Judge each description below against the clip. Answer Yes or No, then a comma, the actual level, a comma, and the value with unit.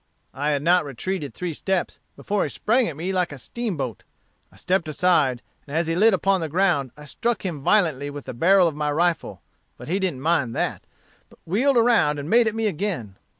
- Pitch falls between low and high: Yes, medium, 170 Hz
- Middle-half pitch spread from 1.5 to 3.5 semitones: No, average, 5.0 semitones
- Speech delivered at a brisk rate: Yes, fast, 210 wpm